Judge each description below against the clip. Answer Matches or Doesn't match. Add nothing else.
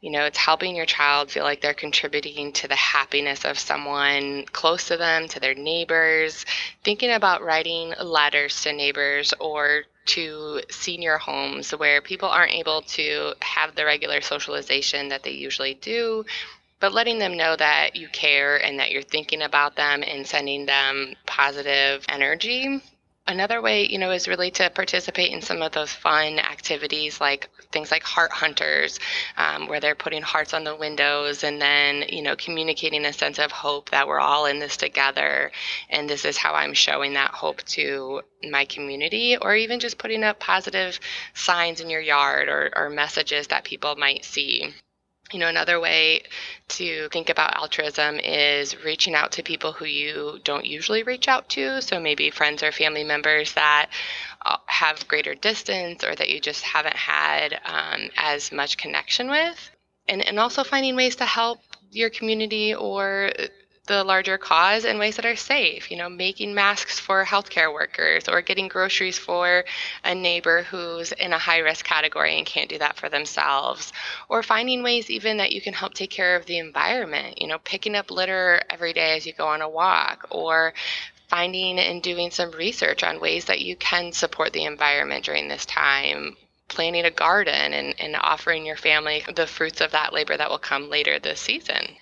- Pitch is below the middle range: Doesn't match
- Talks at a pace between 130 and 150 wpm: Doesn't match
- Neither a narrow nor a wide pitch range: Matches